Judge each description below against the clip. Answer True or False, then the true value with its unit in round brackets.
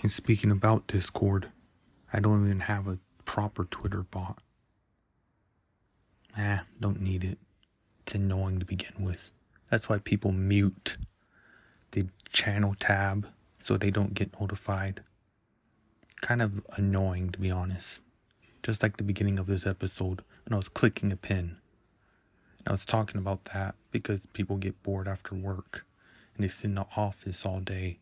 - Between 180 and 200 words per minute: False (155 wpm)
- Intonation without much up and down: True (1.8 semitones)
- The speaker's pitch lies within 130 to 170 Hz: False (100 Hz)